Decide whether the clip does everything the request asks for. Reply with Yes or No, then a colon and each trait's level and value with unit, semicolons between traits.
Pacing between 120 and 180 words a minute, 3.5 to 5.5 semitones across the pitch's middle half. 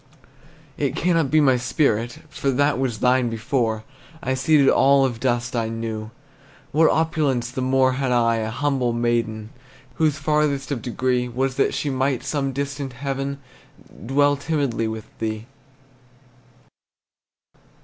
No: average, 140 wpm; average, 3.1 semitones